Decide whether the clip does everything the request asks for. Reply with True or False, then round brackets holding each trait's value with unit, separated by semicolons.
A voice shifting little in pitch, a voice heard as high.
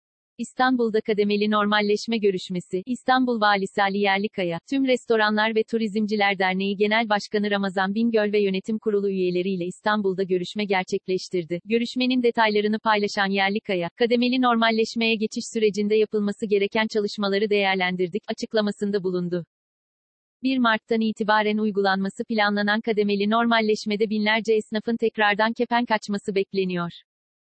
True (2.1 semitones; 210 Hz)